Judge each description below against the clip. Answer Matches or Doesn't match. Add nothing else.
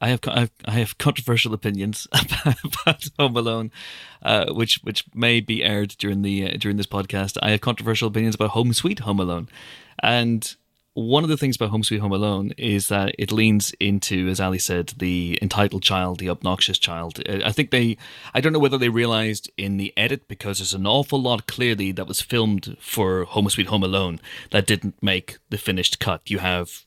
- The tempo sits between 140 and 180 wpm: Doesn't match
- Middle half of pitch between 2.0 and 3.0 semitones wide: Doesn't match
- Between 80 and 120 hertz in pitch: Matches